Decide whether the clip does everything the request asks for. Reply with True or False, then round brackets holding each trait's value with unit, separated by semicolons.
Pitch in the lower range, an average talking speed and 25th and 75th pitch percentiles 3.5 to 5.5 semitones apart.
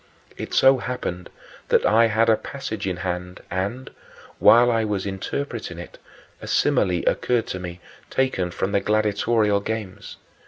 True (105 Hz; 150 wpm; 3.9 semitones)